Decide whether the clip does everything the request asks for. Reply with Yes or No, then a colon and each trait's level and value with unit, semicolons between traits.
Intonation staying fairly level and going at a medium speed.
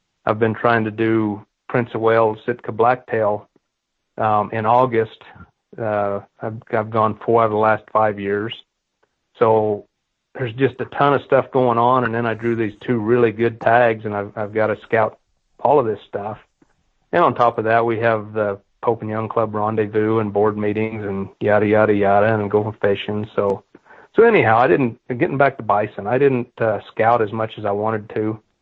Yes: narrow, 1.7 semitones; average, 195 wpm